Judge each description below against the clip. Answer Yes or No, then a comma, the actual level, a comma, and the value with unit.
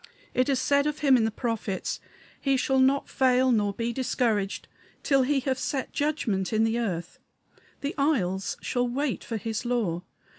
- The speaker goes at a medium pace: Yes, average, 175 wpm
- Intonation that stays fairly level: No, average, 3.6 semitones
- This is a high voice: Yes, high, 245 Hz